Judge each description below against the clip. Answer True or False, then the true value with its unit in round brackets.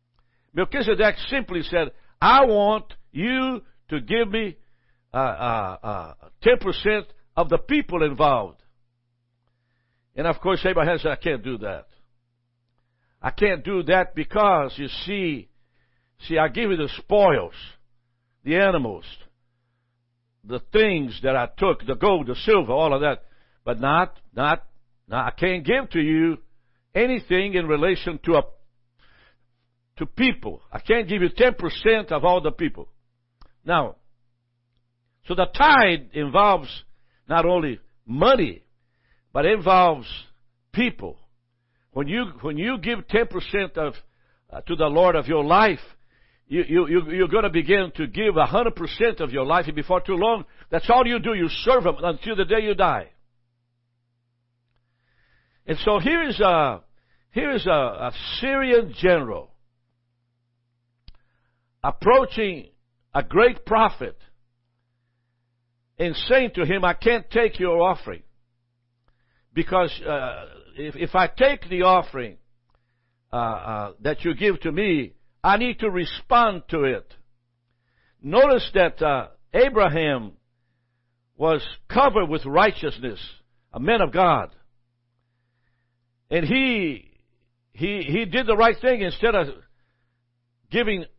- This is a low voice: False (150 Hz)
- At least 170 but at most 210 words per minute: False (135 wpm)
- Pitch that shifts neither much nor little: False (8.2 semitones)